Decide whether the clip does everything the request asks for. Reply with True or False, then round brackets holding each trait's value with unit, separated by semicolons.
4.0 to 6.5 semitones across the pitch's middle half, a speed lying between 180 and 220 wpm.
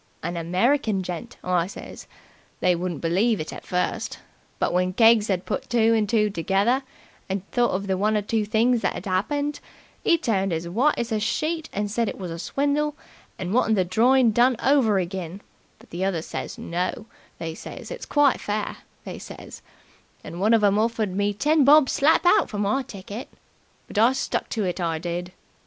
True (4.7 semitones; 190 wpm)